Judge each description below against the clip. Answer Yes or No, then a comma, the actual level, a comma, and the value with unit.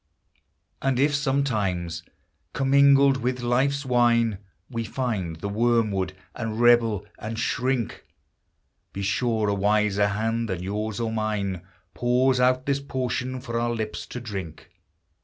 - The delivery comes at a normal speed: No, slow, 130 wpm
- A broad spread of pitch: No, average, 3.7 semitones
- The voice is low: Yes, low, 115 Hz